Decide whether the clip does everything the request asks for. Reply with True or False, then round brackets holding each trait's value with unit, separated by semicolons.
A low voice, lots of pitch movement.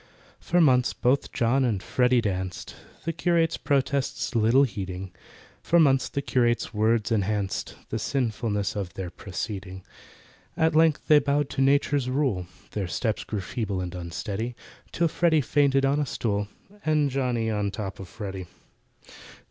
True (120 Hz; 5.7 semitones)